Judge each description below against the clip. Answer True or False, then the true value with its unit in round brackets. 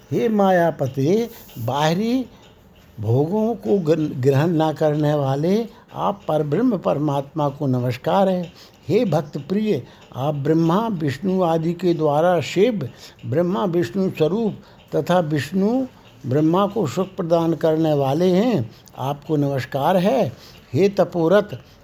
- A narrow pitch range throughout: False (5.3 semitones)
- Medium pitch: True (165 Hz)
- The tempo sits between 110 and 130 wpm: True (120 wpm)